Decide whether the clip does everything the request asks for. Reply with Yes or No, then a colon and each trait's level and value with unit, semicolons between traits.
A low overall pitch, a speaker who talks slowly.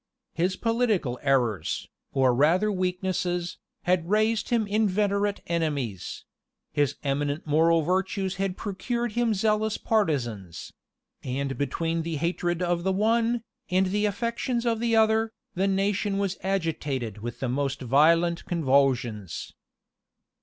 No: medium, 180 Hz; slow, 125 wpm